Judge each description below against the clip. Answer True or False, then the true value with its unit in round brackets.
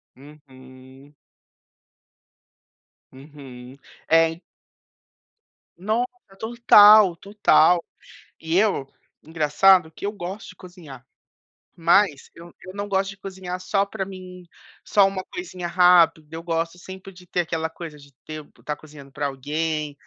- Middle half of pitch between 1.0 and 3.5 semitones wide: False (4.3 semitones)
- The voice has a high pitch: False (170 Hz)